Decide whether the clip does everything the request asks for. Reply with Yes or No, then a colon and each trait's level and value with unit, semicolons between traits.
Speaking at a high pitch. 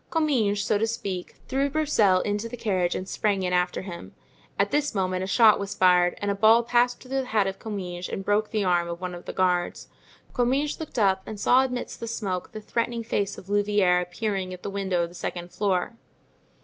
Yes: high, 200 Hz